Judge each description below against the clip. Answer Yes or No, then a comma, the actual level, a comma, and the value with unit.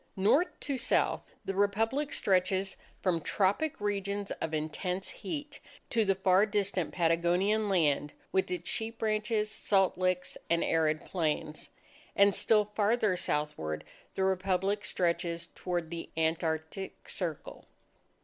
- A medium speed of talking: No, slow, 125 wpm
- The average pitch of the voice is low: No, high, 190 Hz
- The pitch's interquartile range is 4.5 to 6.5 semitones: No, average, 3.6 semitones